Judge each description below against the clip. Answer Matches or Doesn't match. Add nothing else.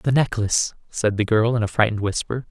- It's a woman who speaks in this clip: Doesn't match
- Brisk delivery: Matches